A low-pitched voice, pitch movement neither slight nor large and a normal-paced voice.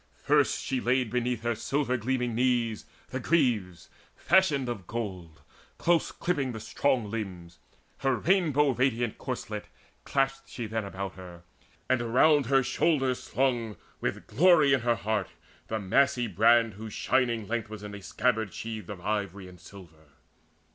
Yes: low, 120 Hz; average, 4.2 semitones; average, 150 wpm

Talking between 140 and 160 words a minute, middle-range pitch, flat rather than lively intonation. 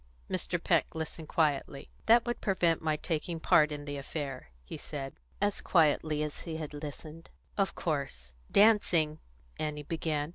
Yes: average, 150 wpm; medium, 155 Hz; narrow, 2.2 semitones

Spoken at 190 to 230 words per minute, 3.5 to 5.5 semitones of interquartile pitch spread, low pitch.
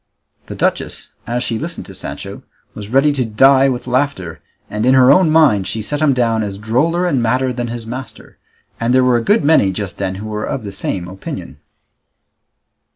Yes: average, 200 wpm; average, 4.1 semitones; low, 120 Hz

